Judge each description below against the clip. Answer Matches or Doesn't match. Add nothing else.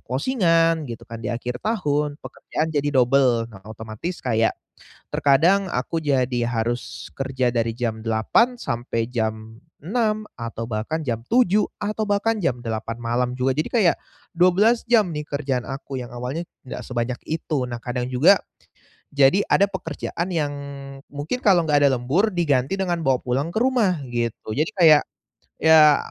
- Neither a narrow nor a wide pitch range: Doesn't match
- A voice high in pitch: Doesn't match